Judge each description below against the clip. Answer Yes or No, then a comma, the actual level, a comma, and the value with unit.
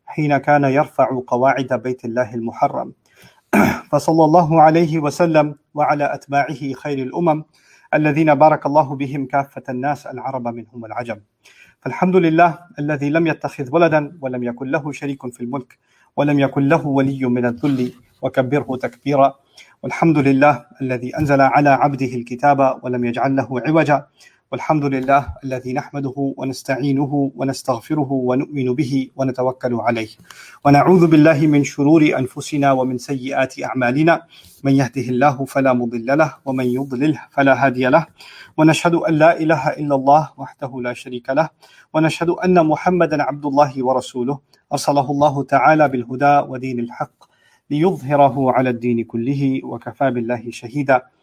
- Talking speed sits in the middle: No, slow, 130 wpm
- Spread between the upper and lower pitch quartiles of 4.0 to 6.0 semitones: No, narrow, 2.6 semitones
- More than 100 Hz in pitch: Yes, medium, 140 Hz